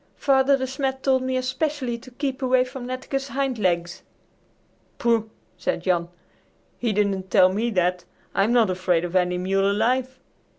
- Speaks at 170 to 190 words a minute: No, average, 160 wpm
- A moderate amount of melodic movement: No, wide, 5.9 semitones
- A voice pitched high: Yes, high, 240 Hz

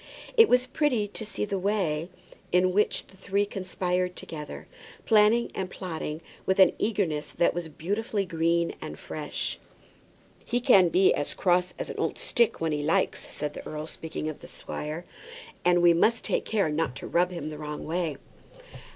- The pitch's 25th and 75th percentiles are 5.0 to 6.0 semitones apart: No, average, 4.1 semitones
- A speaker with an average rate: Yes, average, 180 wpm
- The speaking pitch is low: No, medium, 180 Hz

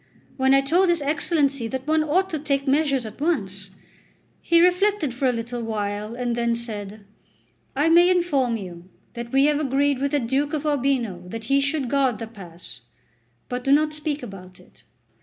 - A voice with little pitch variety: No, average, 4.7 semitones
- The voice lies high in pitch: Yes, very high, 270 Hz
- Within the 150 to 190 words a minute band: Yes, average, 185 wpm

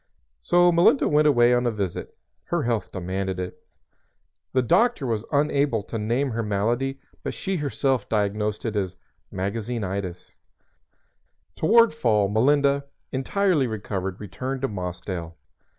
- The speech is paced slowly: Yes, slow, 130 wpm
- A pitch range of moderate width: No, wide, 5.8 semitones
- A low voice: Yes, low, 115 Hz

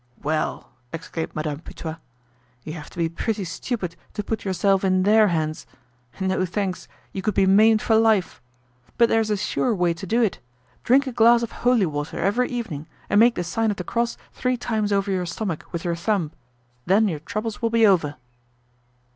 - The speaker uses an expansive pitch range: No, average, 4.8 semitones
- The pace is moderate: Yes, average, 190 wpm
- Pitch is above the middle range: Yes, high, 195 Hz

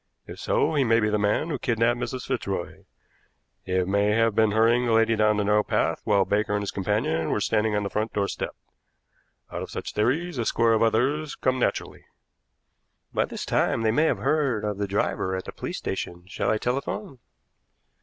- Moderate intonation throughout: Yes, average, 3.0 semitones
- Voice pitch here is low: Yes, low, 110 Hz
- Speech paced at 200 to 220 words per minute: Yes, fast, 205 wpm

